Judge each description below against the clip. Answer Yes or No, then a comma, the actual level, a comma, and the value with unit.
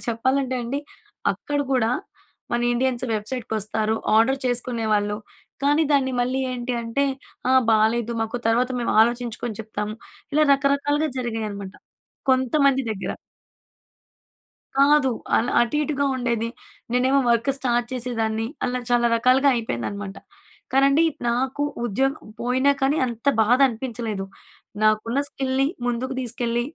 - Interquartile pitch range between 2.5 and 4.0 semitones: Yes, average, 2.9 semitones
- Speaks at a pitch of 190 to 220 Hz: No, high, 245 Hz